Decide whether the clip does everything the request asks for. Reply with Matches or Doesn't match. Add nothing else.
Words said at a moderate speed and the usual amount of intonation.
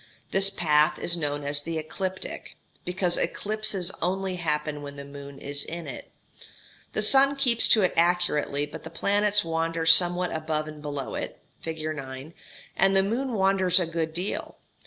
Matches